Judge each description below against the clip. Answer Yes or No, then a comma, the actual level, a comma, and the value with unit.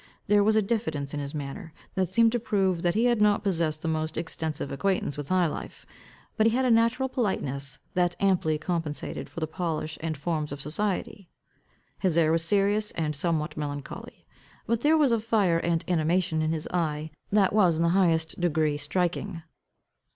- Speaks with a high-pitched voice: No, medium, 170 Hz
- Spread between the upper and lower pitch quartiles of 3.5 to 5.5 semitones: Yes, average, 4.6 semitones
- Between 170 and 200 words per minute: Yes, average, 190 wpm